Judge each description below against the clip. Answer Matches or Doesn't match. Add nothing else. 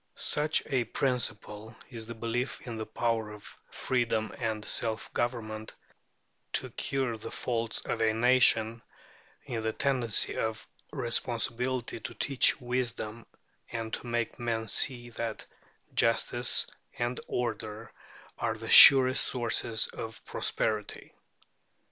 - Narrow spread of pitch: Matches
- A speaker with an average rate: Doesn't match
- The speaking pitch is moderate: Doesn't match